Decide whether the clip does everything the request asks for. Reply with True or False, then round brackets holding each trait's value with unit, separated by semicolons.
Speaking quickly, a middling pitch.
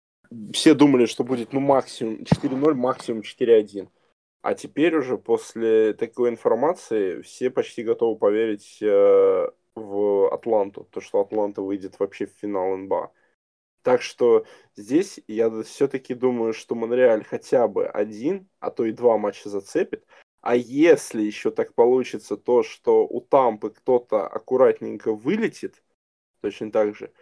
False (135 wpm; 155 Hz)